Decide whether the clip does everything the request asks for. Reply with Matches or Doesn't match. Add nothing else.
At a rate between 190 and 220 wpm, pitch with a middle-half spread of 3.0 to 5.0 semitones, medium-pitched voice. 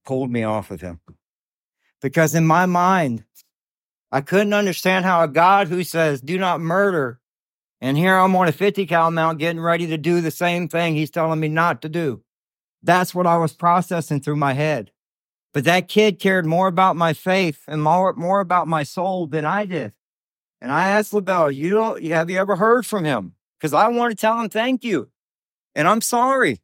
Matches